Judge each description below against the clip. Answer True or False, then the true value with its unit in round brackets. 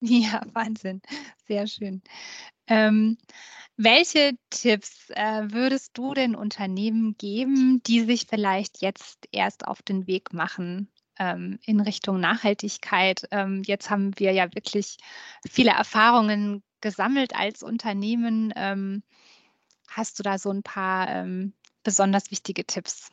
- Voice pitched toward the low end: False (215 Hz)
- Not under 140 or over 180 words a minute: False (125 wpm)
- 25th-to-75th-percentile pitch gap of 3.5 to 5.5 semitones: False (3.1 semitones)